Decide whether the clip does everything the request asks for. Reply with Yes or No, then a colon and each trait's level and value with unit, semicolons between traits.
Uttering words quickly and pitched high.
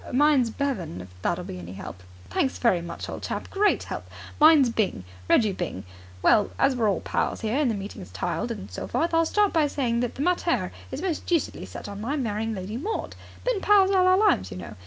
Yes: fast, 220 wpm; high, 245 Hz